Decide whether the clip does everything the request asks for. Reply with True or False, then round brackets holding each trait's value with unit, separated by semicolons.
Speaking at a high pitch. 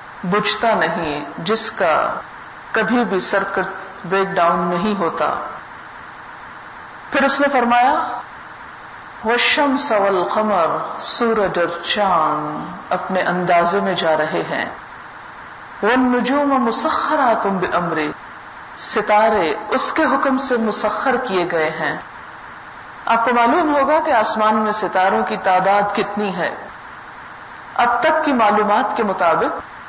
True (215 Hz)